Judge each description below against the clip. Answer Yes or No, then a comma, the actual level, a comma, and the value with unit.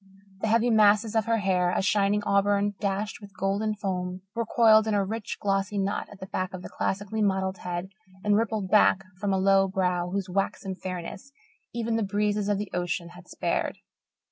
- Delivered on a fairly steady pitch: Yes, narrow, 1.9 semitones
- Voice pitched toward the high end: Yes, high, 200 Hz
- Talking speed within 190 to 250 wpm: Yes, average, 195 wpm